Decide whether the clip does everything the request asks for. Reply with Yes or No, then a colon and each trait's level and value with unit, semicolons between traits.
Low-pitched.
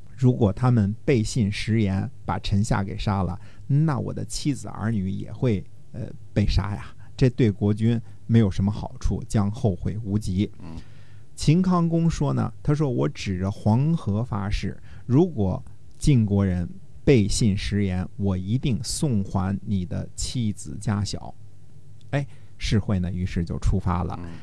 Yes: low, 105 Hz